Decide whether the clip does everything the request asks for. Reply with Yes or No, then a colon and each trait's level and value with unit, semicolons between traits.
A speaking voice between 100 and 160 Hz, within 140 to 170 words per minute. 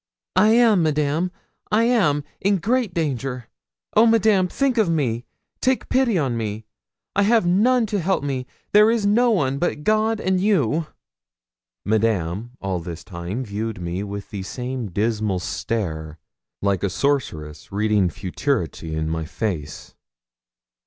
Yes: low, 135 Hz; average, 145 wpm